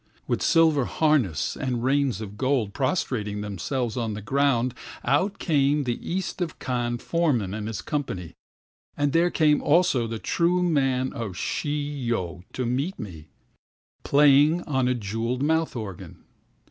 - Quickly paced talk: No, slow, 135 wpm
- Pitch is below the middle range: Yes, low, 130 Hz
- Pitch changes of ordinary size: Yes, average, 4.8 semitones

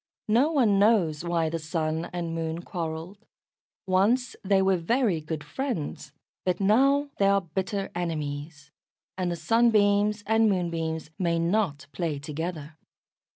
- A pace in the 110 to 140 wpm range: Yes, slow, 135 wpm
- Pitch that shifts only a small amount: No, average, 4.3 semitones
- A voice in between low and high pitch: Yes, medium, 175 Hz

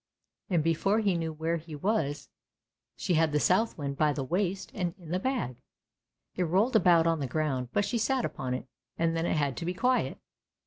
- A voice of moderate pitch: Yes, medium, 165 Hz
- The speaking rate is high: Yes, fast, 210 wpm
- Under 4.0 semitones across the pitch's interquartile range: No, average, 4.5 semitones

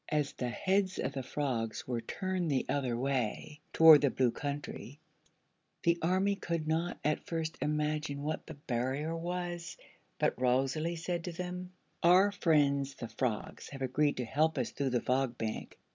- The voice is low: No, medium, 150 Hz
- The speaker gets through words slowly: No, average, 165 wpm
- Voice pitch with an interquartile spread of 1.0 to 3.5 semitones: No, average, 4.4 semitones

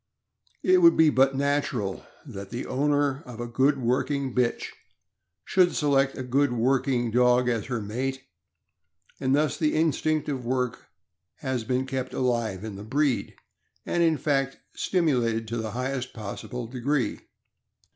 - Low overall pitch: Yes, low, 130 Hz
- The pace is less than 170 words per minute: Yes, average, 145 wpm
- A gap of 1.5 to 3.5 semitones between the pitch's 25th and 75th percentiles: Yes, average, 3.0 semitones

